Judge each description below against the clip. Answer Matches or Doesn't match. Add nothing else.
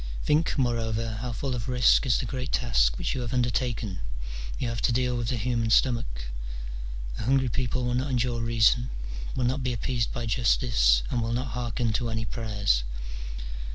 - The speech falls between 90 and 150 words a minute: Doesn't match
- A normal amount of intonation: Doesn't match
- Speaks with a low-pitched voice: Matches